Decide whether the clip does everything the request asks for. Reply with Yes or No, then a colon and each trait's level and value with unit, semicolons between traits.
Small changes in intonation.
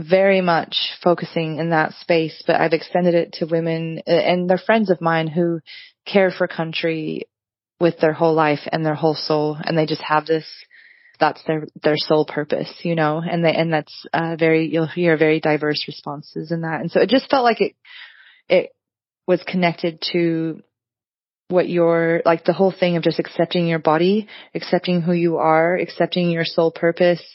Yes: narrow, 2.0 semitones